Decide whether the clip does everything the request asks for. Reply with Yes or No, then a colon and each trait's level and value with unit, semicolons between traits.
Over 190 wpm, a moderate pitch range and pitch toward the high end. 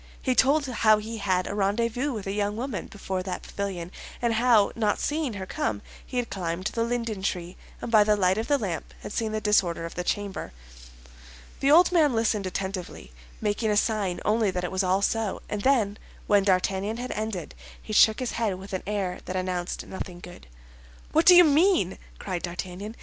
Yes: average, 200 wpm; average, 3.7 semitones; high, 205 Hz